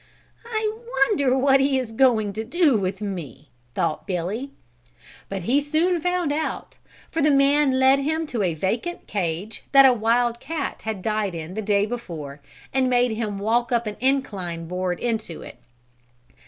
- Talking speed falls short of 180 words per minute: Yes, average, 170 wpm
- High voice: Yes, high, 235 Hz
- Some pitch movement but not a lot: No, wide, 5.8 semitones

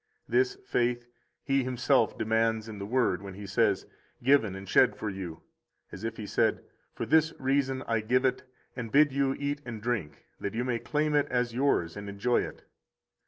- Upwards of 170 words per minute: Yes, average, 190 wpm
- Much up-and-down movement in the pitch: No, average, 4.3 semitones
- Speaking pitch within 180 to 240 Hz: No, low, 120 Hz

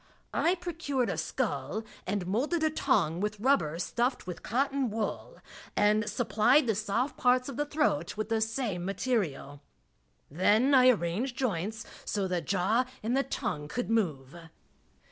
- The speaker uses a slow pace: No, average, 150 wpm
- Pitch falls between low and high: No, high, 220 Hz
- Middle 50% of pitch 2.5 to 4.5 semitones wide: No, wide, 5.6 semitones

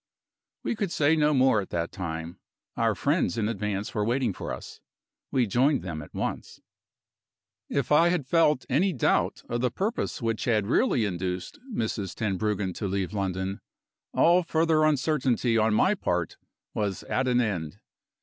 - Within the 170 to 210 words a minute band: No, average, 160 wpm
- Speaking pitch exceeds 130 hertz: No, low, 115 Hz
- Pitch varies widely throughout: Yes, wide, 7.3 semitones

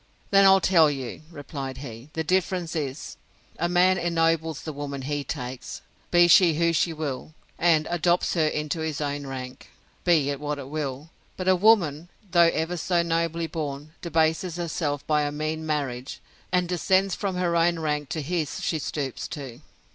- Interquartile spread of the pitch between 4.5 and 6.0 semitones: No, average, 3.1 semitones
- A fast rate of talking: No, average, 175 wpm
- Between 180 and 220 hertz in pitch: No, medium, 160 Hz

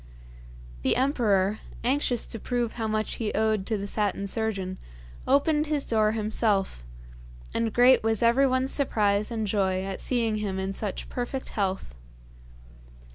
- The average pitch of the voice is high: Yes, high, 220 Hz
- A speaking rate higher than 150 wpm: No, average, 140 wpm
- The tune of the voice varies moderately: Yes, average, 3.4 semitones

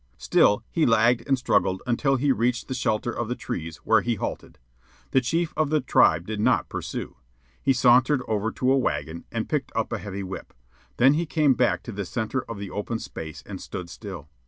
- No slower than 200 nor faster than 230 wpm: Yes, fast, 205 wpm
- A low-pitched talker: Yes, low, 115 Hz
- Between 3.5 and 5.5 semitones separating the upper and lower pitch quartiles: Yes, average, 4.7 semitones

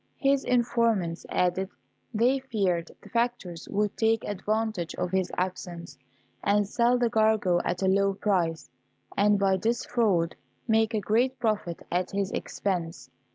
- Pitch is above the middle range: Yes, high, 205 Hz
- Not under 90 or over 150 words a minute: Yes, average, 145 wpm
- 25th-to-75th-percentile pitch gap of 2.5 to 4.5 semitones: Yes, average, 3.9 semitones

